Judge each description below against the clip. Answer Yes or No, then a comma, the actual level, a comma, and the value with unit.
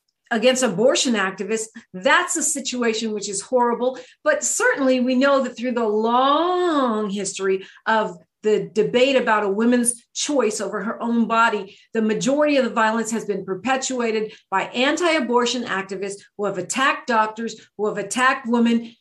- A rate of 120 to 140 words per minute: No, average, 155 wpm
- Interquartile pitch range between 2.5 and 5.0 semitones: Yes, average, 3.4 semitones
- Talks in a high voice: Yes, high, 230 Hz